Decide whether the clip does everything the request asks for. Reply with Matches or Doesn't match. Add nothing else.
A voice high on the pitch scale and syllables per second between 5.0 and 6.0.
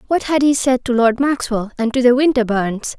Matches